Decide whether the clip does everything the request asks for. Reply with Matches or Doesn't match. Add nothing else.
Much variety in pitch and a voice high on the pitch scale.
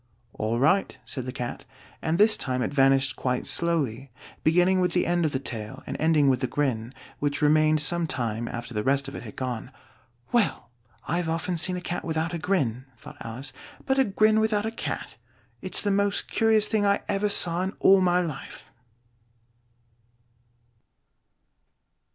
Doesn't match